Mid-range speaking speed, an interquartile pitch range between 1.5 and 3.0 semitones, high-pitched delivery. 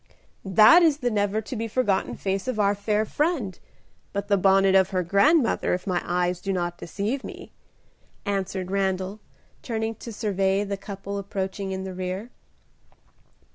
Yes: average, 160 wpm; narrow, 2.4 semitones; high, 200 Hz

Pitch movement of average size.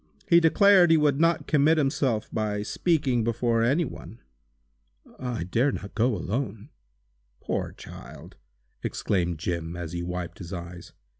No: wide, 8.3 semitones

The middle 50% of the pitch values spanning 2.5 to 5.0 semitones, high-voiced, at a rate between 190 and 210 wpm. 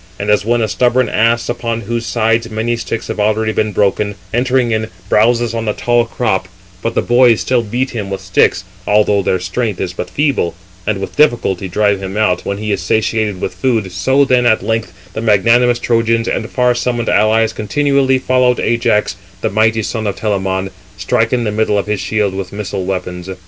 No: average, 2.9 semitones; low, 110 Hz; average, 195 wpm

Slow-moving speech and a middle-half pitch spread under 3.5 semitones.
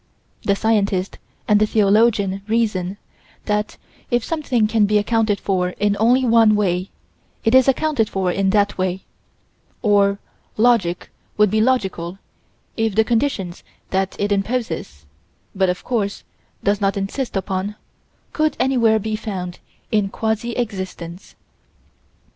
Yes: slow, 130 wpm; average, 2.8 semitones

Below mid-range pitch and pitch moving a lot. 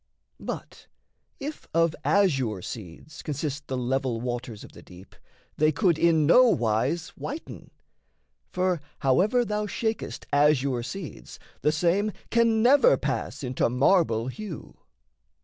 No: medium, 155 Hz; wide, 7.8 semitones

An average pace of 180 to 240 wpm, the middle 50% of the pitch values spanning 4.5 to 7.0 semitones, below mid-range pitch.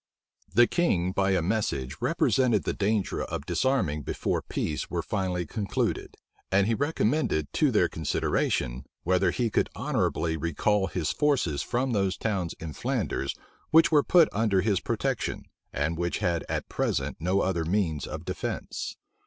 No: average, 155 wpm; average, 5.2 semitones; very low, 95 Hz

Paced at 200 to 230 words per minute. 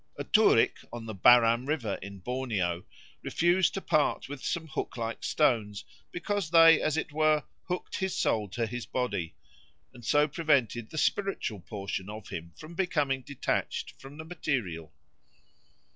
No: average, 155 wpm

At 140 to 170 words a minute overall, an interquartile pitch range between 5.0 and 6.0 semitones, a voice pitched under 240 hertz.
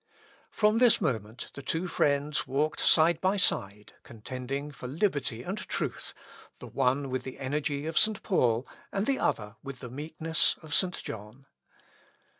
No: average, 160 wpm; average, 4.6 semitones; medium, 140 Hz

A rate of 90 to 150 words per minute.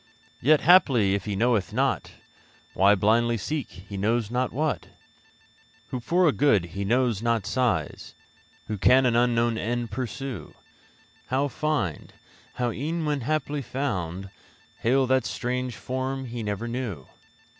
Yes: average, 140 wpm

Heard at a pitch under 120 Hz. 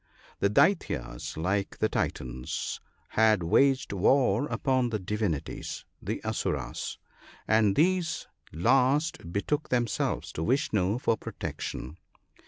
Yes: low, 110 Hz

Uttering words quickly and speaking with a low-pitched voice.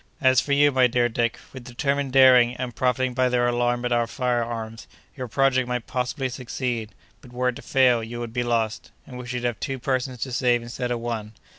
Yes: fast, 225 wpm; low, 125 Hz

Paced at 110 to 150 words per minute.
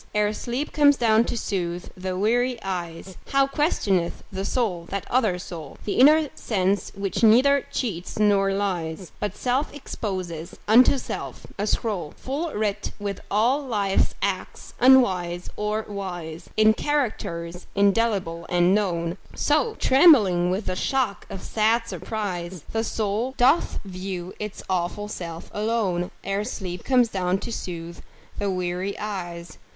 Yes: average, 140 wpm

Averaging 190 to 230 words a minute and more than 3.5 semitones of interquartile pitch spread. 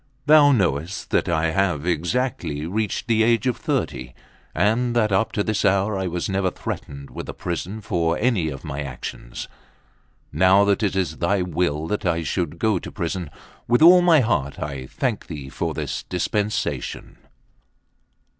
No: average, 165 wpm; average, 5.2 semitones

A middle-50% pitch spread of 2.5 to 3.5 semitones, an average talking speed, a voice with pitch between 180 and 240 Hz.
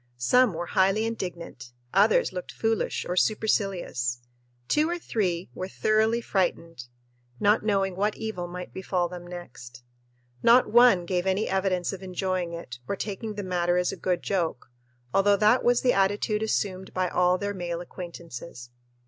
Yes: average, 3.2 semitones; average, 155 wpm; medium, 185 Hz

